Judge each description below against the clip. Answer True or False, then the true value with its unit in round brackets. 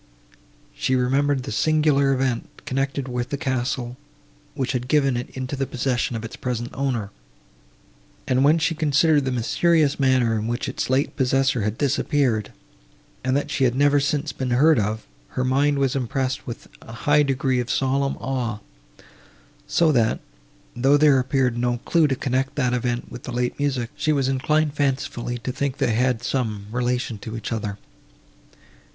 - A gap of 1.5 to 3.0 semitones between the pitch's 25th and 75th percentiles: True (2.5 semitones)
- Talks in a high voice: False (130 Hz)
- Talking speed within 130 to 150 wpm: False (170 wpm)